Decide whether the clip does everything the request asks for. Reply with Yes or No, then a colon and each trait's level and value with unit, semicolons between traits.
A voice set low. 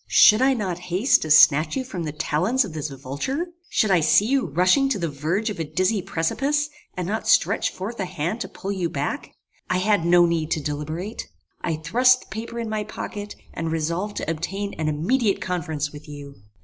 No: medium, 180 Hz